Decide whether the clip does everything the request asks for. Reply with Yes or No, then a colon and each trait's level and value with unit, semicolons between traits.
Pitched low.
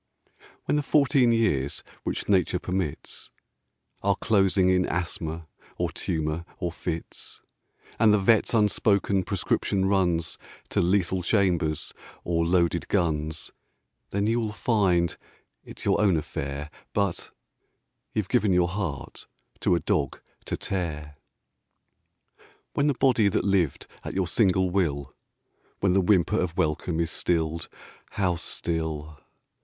Yes: very low, 90 Hz